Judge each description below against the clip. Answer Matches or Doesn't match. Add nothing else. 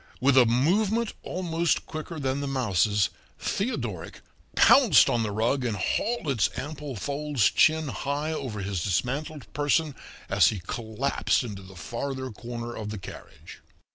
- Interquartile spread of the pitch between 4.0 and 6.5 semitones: Matches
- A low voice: Matches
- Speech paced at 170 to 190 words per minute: Doesn't match